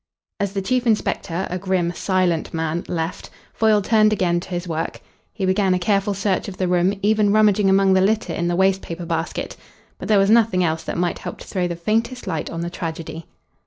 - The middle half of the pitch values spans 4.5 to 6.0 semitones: No, average, 3.0 semitones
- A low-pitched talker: No, medium, 185 Hz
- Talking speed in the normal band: No, fast, 215 wpm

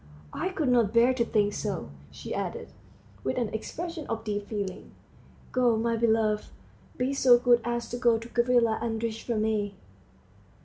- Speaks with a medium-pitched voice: No, high, 230 Hz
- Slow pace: No, average, 165 wpm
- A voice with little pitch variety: Yes, narrow, 1.9 semitones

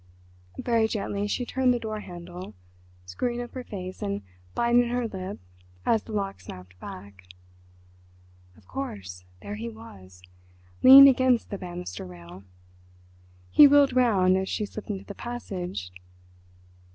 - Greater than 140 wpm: No, slow, 135 wpm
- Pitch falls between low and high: No, high, 195 Hz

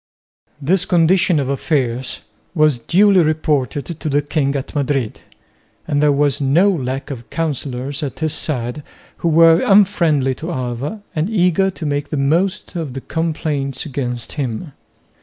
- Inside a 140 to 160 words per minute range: Yes, average, 150 wpm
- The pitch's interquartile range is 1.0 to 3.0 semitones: No, average, 3.5 semitones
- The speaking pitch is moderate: Yes, medium, 150 Hz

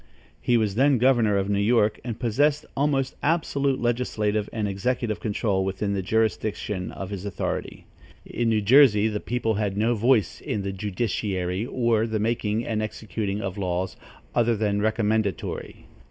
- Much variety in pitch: No, average, 2.8 semitones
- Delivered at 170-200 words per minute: No, average, 155 wpm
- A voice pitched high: No, low, 110 Hz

